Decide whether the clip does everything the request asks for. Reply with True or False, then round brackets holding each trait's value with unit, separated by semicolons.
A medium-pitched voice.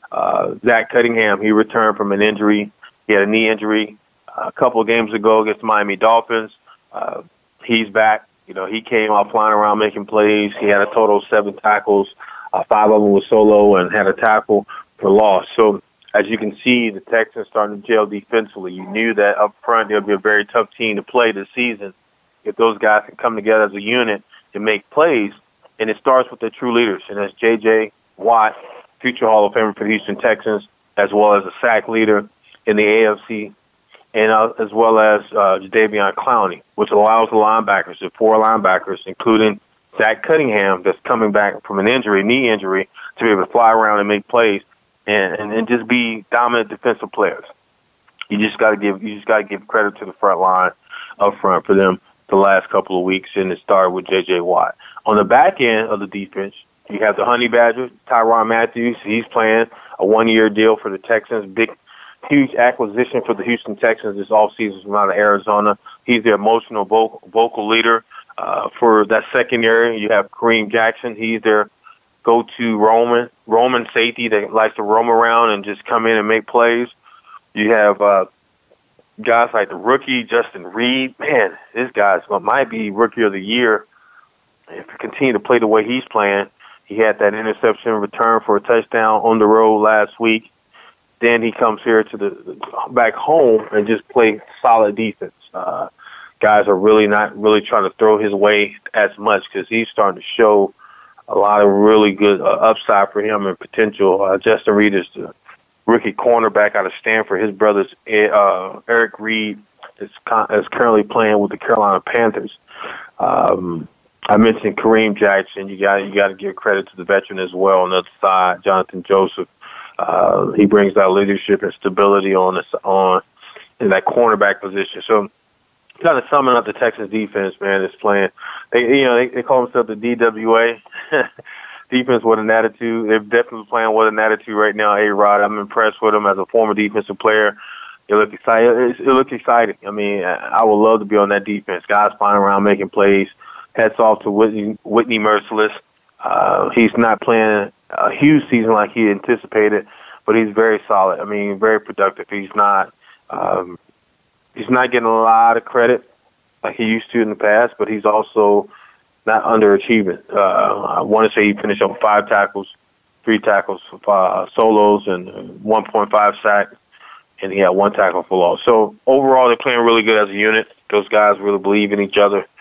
False (110 Hz)